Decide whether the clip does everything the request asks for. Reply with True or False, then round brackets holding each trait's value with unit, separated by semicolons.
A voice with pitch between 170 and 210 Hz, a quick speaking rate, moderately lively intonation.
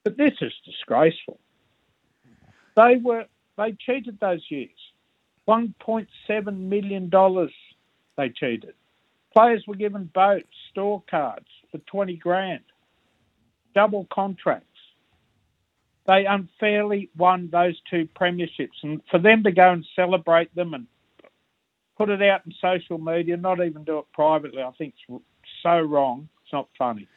False (185 Hz; 135 wpm; 3.7 semitones)